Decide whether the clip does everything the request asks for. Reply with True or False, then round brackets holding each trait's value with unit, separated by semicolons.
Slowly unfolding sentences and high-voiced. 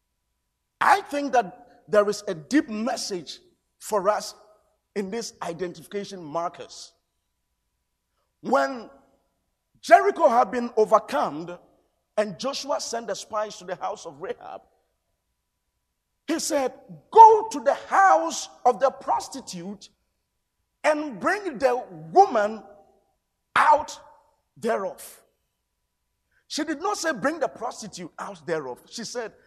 True (110 wpm; 220 Hz)